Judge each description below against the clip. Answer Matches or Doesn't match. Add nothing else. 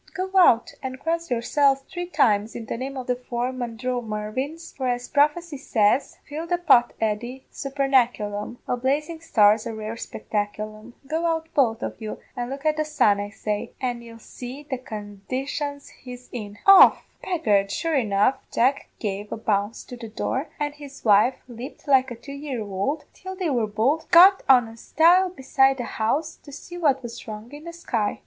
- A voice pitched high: Matches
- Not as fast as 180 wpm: Doesn't match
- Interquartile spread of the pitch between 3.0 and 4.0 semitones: Doesn't match